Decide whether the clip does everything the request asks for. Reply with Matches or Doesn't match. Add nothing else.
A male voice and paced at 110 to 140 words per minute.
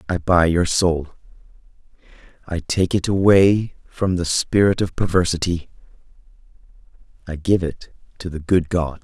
Matches